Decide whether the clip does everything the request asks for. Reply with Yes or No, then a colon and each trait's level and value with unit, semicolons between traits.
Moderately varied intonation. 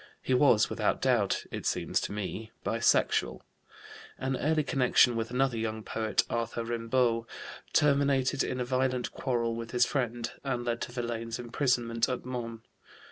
No: narrow, 2.1 semitones